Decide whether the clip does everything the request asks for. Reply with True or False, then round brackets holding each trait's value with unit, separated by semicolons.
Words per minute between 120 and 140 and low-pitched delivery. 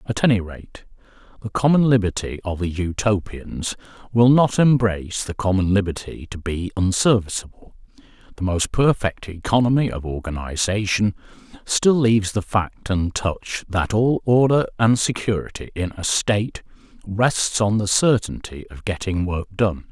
True (135 wpm; 100 Hz)